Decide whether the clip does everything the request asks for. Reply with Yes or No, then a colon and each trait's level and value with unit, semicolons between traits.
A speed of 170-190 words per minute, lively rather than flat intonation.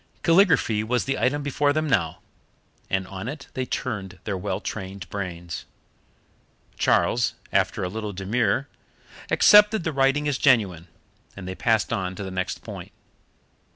No: average, 150 wpm; wide, 6.4 semitones